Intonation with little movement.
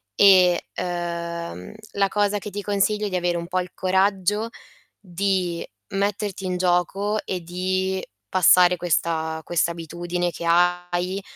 Yes: narrow, 2.1 semitones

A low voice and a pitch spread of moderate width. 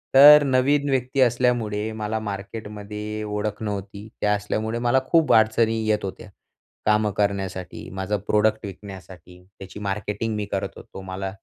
No: low, 105 Hz; narrow, 2.2 semitones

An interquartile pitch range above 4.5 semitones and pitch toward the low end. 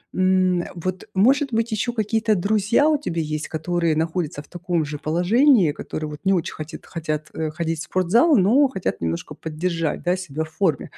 No: average, 5.1 semitones; medium, 175 Hz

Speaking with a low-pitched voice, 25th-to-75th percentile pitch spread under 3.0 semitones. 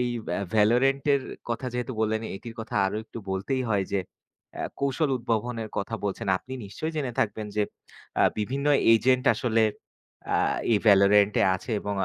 No: low, 115 Hz; average, 3.6 semitones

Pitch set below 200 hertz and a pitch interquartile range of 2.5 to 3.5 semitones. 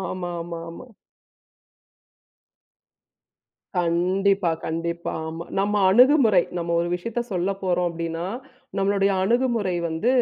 Yes: medium, 185 Hz; average, 2.9 semitones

